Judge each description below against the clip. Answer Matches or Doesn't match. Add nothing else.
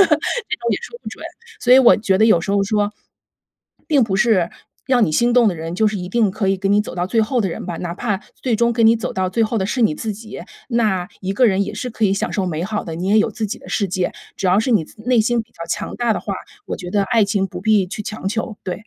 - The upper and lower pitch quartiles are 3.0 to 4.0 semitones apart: Matches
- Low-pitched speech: Doesn't match